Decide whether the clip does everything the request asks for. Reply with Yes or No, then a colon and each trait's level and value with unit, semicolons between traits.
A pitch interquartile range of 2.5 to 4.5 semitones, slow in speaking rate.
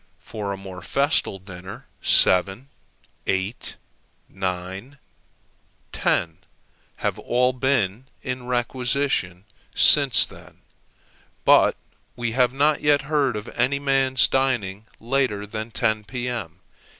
No: average, 5.3 semitones; slow, 105 wpm